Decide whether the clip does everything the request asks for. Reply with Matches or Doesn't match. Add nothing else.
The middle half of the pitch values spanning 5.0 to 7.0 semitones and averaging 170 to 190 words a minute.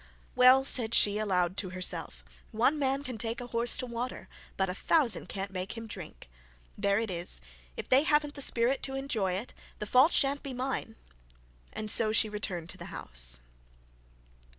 Matches